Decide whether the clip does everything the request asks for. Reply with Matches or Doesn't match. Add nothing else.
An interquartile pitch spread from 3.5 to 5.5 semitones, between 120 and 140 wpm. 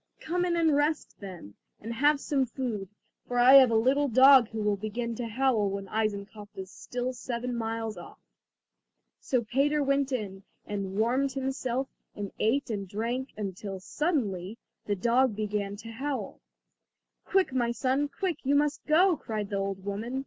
Doesn't match